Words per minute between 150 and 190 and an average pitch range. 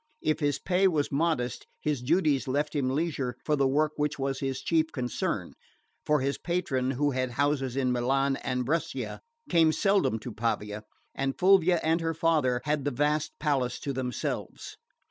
Yes: average, 170 wpm; average, 3.4 semitones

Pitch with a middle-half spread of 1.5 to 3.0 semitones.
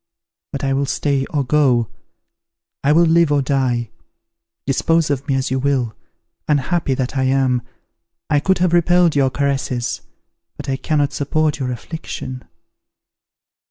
Yes: narrow, 2.5 semitones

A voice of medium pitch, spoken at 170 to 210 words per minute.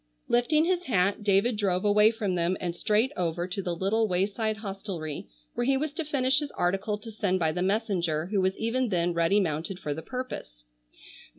No: high, 200 Hz; average, 195 wpm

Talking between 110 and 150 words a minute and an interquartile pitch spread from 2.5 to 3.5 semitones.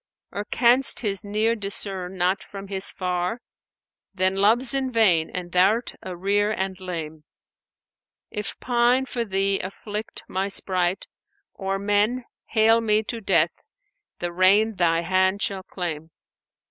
Yes: average, 145 wpm; average, 3.0 semitones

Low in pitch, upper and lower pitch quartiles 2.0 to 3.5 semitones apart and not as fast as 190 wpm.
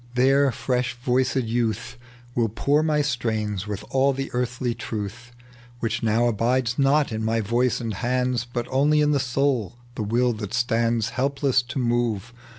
Yes: low, 120 Hz; narrow, 2.5 semitones; average, 160 wpm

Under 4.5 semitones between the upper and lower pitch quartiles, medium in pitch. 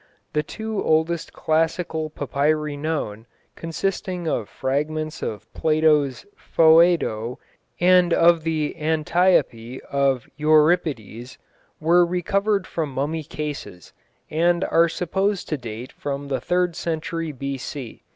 Yes: average, 3.5 semitones; medium, 155 Hz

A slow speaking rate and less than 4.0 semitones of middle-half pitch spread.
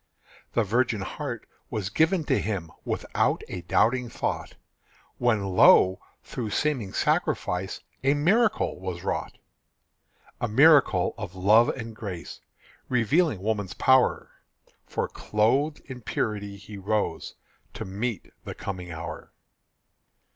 No: slow, 120 wpm; average, 5.1 semitones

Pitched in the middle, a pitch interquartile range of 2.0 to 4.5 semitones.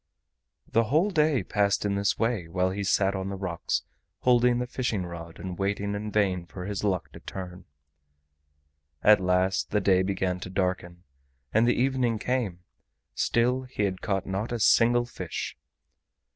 No: low, 100 Hz; average, 4.2 semitones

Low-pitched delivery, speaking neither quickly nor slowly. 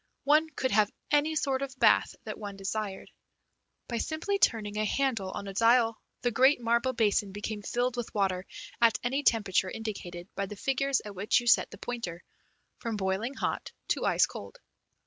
No: high, 230 Hz; average, 180 wpm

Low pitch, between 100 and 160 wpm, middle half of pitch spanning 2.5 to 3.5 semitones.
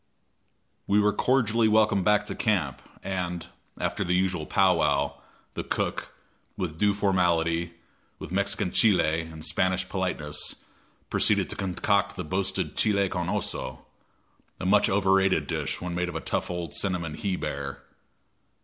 Yes: very low, 90 Hz; average, 145 wpm; average, 3.2 semitones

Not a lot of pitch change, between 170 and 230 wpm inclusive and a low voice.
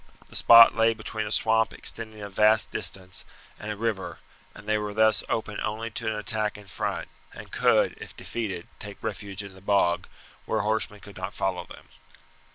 Yes: narrow, 1.7 semitones; average, 185 wpm; low, 105 Hz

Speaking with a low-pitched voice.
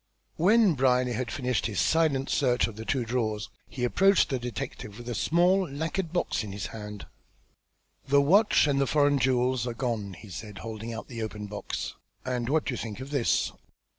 Yes: low, 125 Hz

